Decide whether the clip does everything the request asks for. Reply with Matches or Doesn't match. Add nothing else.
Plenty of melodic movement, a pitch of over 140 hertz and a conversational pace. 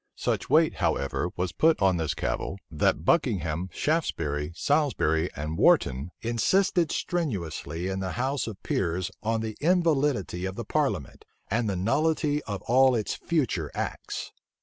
Doesn't match